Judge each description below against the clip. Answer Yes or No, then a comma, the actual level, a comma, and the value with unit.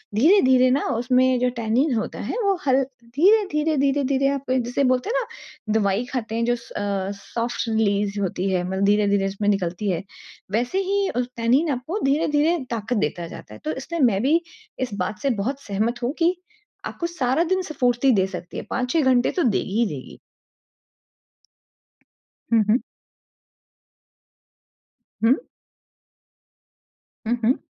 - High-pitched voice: Yes, high, 245 Hz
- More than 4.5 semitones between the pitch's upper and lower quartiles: Yes, average, 5.1 semitones